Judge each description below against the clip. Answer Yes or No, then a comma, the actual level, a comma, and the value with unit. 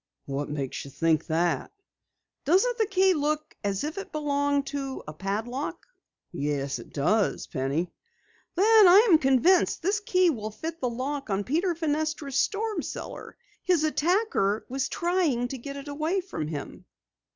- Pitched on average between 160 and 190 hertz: No, very high, 285 Hz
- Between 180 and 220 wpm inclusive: No, average, 155 wpm